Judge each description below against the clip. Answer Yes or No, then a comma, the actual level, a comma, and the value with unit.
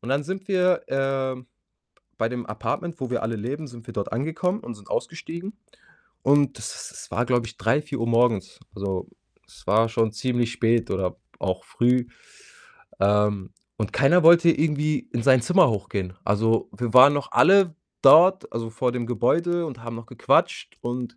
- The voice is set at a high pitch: No, low, 125 Hz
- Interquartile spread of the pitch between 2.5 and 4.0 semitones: No, average, 4.9 semitones